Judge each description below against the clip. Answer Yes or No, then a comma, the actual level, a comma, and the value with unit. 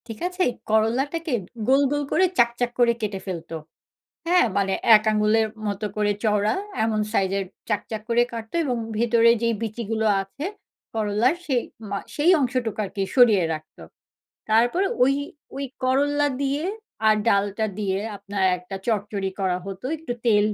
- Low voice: No, high, 225 Hz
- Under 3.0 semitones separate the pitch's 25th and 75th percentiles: No, average, 3.7 semitones